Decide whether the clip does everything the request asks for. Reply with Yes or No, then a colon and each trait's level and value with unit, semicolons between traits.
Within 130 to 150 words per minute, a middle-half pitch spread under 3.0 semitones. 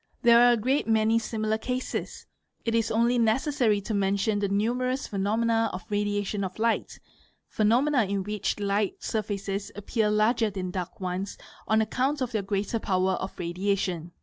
No: average, 160 wpm; narrow, 2.6 semitones